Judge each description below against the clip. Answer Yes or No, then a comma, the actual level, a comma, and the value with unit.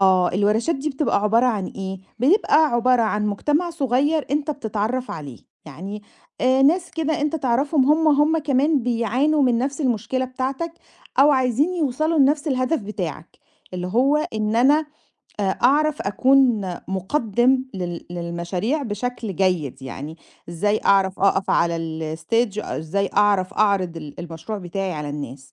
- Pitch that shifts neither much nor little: No, wide, 6.6 semitones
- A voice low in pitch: No, high, 235 Hz